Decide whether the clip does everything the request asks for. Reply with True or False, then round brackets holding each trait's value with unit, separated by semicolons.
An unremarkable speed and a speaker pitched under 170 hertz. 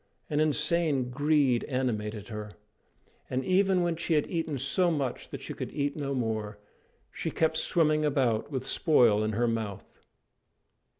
True (155 wpm; 140 Hz)